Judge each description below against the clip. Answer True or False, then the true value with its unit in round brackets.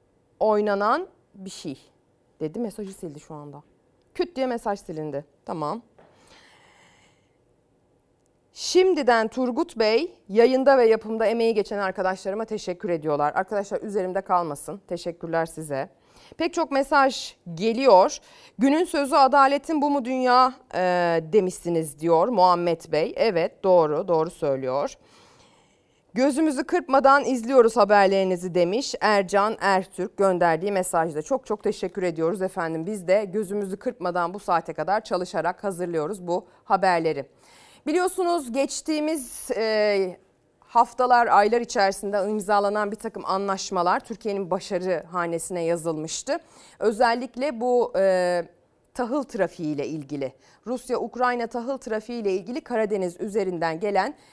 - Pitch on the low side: False (205 Hz)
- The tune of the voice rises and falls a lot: True (5.7 semitones)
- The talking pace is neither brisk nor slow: True (110 wpm)